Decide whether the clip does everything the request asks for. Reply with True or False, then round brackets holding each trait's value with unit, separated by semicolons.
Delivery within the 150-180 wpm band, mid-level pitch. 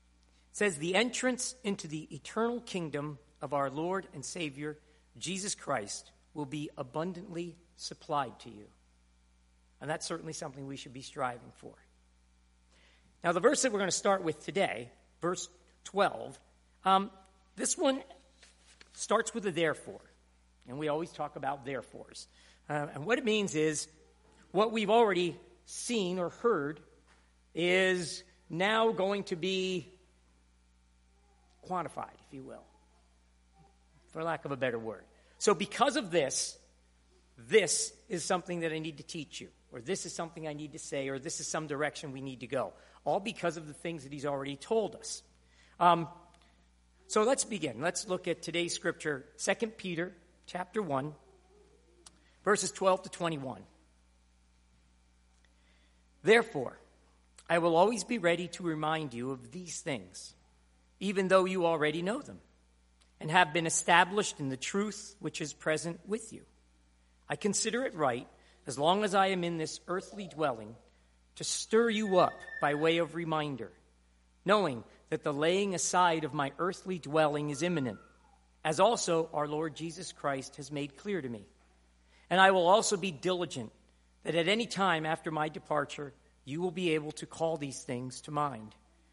True (160 wpm; 155 Hz)